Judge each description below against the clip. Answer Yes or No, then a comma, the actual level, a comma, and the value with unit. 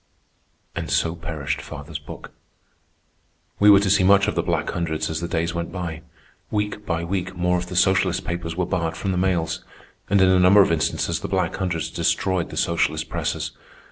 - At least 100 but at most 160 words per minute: No, average, 195 wpm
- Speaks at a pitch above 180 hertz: No, very low, 90 Hz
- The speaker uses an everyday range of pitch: No, narrow, 2.2 semitones